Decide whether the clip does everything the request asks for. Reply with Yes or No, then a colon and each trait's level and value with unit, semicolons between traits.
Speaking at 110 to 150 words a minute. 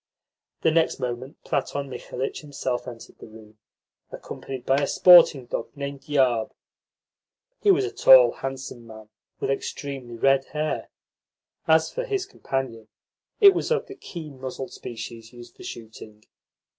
Yes: average, 145 wpm